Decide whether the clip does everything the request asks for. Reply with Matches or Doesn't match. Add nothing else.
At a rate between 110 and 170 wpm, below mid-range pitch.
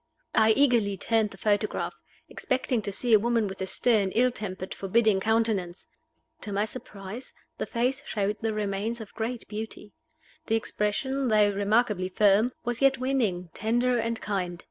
Doesn't match